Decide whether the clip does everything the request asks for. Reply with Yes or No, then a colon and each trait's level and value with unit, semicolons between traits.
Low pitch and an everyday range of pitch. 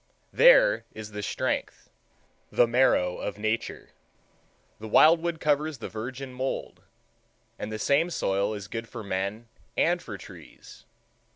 No: low, 115 Hz; wide, 5.7 semitones